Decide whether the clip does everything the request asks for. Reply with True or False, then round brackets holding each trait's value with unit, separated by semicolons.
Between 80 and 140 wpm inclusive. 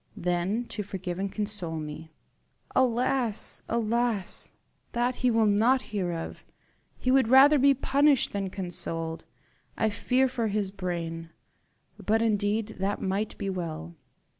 True (135 wpm)